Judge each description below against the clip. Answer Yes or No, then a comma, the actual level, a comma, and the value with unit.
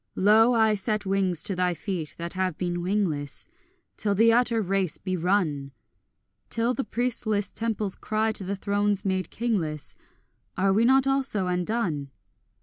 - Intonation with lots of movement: No, average, 3.6 semitones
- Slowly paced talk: No, average, 150 wpm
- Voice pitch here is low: No, high, 200 Hz